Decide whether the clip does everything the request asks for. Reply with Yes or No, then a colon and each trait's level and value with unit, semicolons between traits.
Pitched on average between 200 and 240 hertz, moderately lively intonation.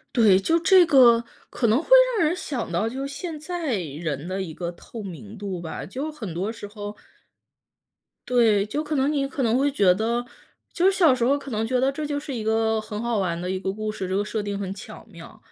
No: high, 225 Hz; wide, 5.8 semitones